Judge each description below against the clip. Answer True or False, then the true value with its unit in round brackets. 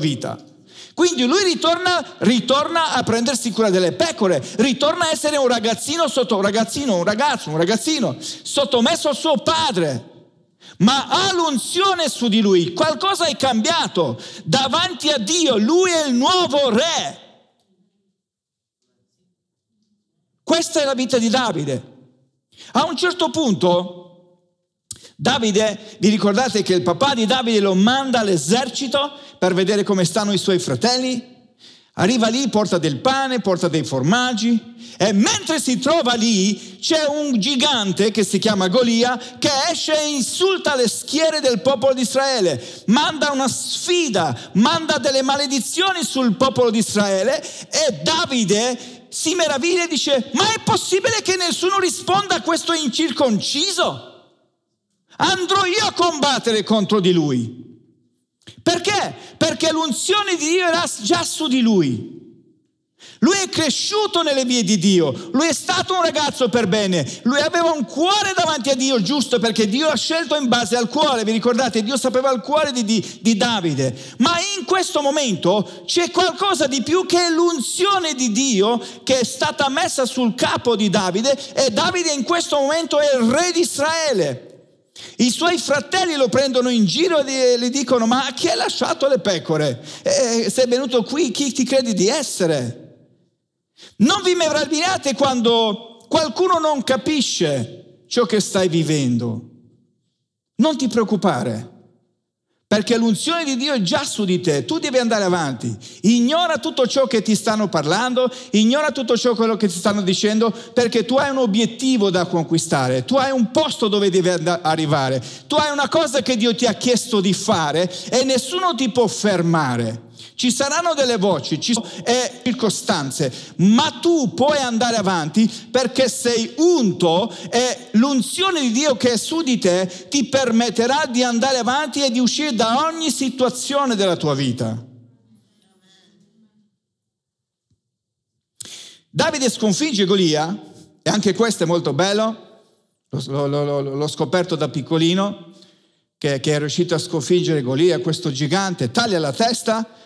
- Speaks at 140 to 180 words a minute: True (150 wpm)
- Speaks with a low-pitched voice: False (245 Hz)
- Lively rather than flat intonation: True (7.3 semitones)